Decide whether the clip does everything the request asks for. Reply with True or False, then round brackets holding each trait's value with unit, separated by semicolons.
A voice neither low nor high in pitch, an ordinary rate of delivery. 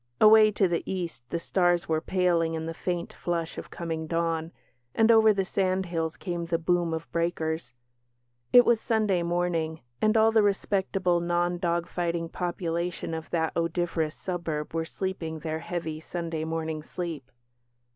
True (170 Hz; 155 wpm)